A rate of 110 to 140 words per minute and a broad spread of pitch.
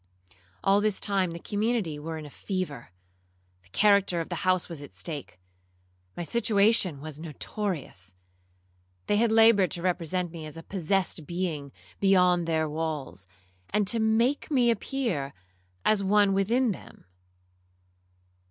Yes: slow, 135 wpm; wide, 5.8 semitones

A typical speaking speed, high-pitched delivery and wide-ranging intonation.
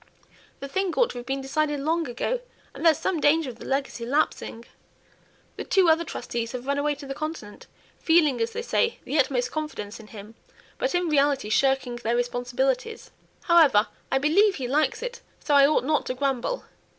No: average, 190 wpm; very high, 280 Hz; average, 4.6 semitones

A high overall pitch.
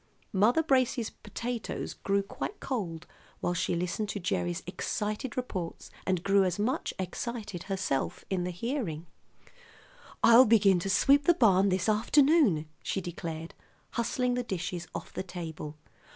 Yes: high, 195 Hz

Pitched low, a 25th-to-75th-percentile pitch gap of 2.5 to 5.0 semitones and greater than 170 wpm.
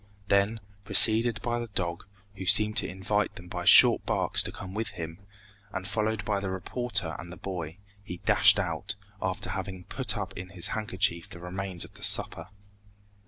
Yes: very low, 95 Hz; average, 3.0 semitones; average, 180 wpm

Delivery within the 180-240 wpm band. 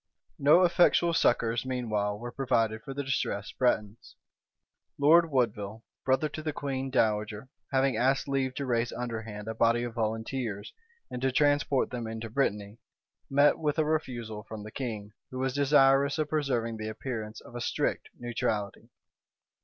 No: average, 155 wpm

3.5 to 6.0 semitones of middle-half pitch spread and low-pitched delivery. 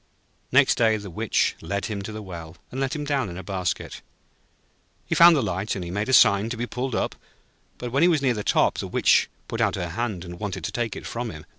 Yes: average, 4.8 semitones; low, 105 Hz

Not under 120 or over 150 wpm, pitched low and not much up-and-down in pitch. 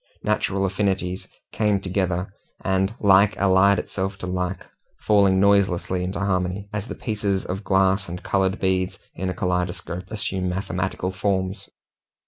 Yes: slow, 135 wpm; very low, 95 Hz; narrow, 1.3 semitones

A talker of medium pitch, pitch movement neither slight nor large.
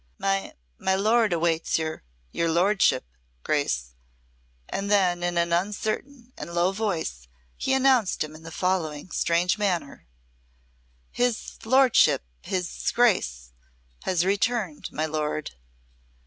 Yes: medium, 180 Hz; average, 4.6 semitones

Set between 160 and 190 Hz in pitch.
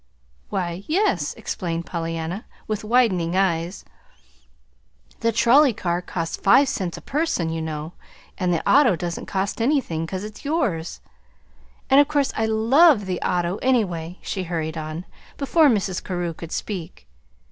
Yes: medium, 185 Hz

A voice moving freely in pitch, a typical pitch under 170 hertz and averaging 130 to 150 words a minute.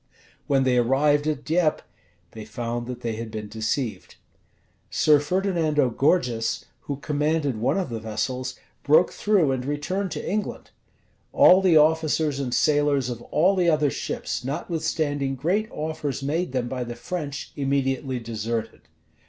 No: average, 4.2 semitones; medium, 140 Hz; average, 145 wpm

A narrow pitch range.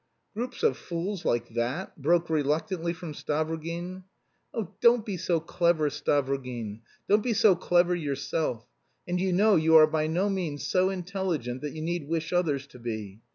No: average, 4.0 semitones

